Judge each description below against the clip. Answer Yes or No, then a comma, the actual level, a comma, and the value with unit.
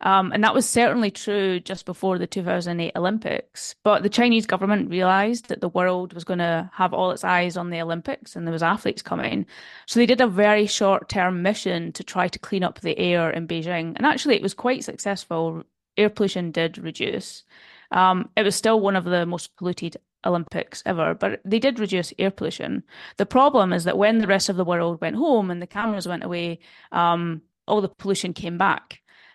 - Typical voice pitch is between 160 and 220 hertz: Yes, high, 190 Hz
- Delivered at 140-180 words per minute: No, fast, 205 wpm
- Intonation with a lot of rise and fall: No, average, 3.2 semitones